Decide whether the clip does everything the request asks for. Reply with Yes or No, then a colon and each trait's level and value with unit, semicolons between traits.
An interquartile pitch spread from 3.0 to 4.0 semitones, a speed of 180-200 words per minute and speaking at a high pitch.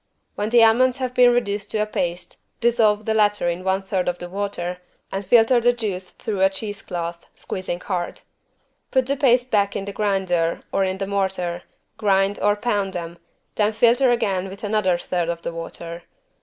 Yes: average, 3.6 semitones; average, 190 wpm; high, 200 Hz